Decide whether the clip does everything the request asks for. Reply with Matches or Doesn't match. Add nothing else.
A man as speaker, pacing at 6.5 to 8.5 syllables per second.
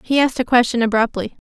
Doesn't match